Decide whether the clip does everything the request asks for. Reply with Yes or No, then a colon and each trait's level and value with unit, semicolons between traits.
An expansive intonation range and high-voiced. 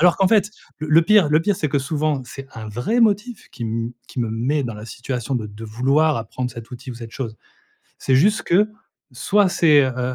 No: wide, 5.9 semitones; low, 135 Hz